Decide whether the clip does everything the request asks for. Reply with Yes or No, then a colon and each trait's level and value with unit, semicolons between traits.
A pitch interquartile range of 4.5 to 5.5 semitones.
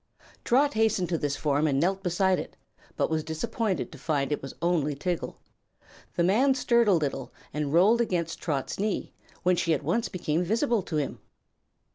Yes: average, 5.2 semitones